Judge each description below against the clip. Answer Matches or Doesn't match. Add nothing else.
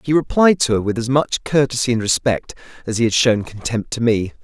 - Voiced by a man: Matches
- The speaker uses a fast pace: Matches